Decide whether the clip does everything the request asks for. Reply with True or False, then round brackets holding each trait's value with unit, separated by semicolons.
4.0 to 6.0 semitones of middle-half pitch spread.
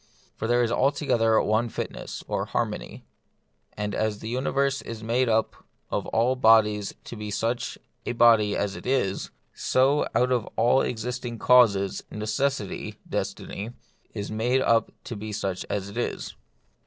False (2.8 semitones)